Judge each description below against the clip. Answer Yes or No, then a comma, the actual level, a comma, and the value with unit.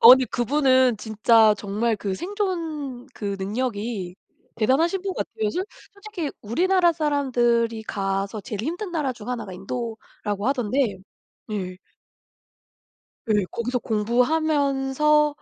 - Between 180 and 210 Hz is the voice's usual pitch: No, high, 245 Hz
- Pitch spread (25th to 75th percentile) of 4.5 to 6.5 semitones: Yes, wide, 5.9 semitones